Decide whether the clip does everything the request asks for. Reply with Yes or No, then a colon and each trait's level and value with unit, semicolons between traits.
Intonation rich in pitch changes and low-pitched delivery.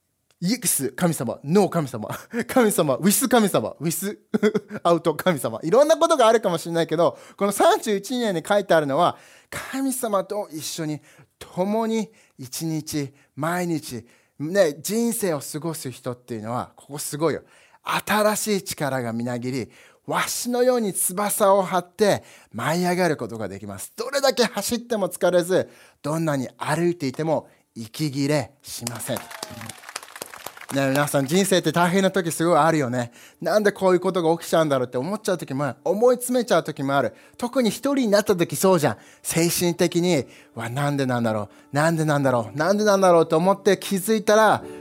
No: wide, 6.4 semitones; medium, 170 Hz